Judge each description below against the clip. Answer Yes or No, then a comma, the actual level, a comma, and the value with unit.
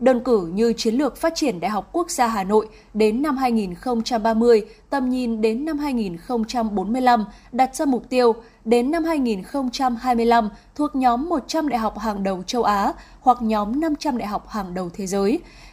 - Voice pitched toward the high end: Yes, high, 235 Hz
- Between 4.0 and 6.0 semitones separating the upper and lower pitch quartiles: No, average, 3.2 semitones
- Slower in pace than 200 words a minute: Yes, average, 175 wpm